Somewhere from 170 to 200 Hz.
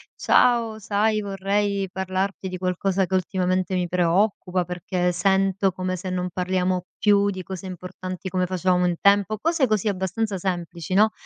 Yes: high, 190 Hz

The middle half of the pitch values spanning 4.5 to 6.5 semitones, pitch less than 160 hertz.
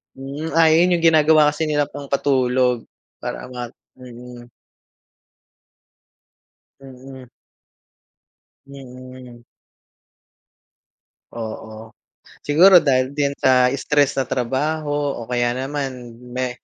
No: average, 2.9 semitones; low, 135 Hz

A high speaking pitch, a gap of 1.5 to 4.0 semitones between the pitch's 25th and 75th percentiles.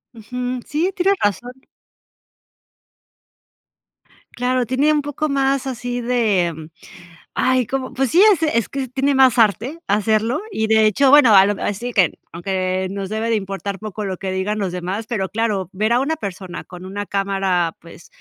No: high, 220 Hz; average, 4.9 semitones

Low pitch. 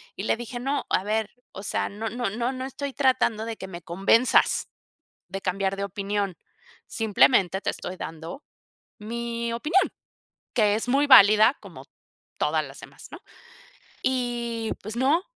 No: high, 225 Hz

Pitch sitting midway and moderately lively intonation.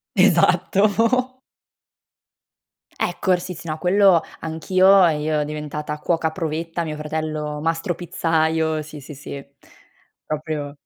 Yes: medium, 160 Hz; average, 3.0 semitones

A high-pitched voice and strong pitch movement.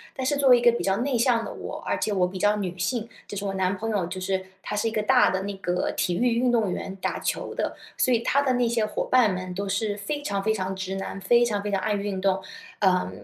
No: high, 205 Hz; average, 3.7 semitones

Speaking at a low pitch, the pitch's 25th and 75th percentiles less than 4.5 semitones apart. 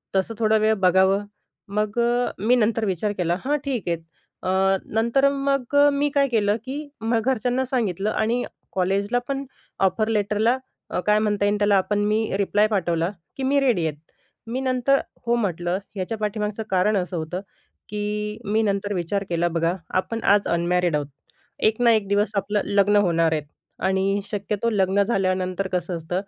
No: high, 205 Hz; average, 3.4 semitones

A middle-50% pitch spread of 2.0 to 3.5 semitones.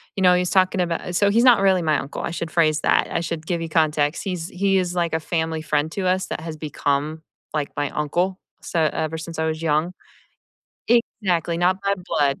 Yes: average, 2.7 semitones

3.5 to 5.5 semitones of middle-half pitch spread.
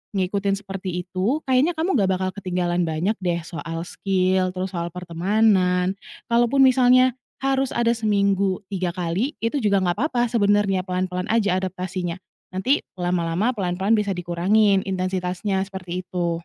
No: average, 2.7 semitones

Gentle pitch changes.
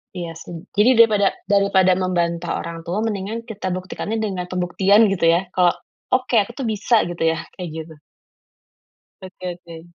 No: average, 3.2 semitones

